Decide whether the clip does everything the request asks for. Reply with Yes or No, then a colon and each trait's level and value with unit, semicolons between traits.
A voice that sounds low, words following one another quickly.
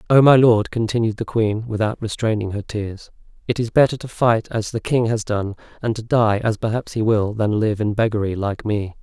Yes: low, 110 Hz; fast, 220 wpm